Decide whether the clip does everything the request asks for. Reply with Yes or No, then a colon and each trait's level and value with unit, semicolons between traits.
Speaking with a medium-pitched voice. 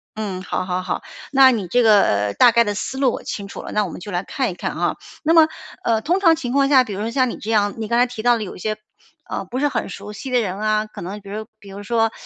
No: high, 220 Hz